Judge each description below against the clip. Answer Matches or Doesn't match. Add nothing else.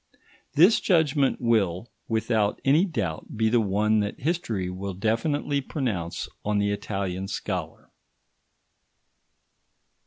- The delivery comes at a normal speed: Doesn't match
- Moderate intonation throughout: Doesn't match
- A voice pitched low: Matches